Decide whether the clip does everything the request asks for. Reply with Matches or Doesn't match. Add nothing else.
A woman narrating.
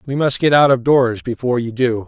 Doesn't match